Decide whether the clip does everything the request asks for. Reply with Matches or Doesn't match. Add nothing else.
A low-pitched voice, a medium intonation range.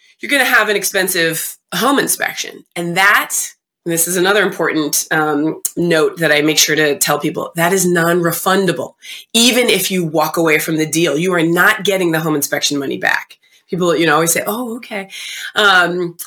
Doesn't match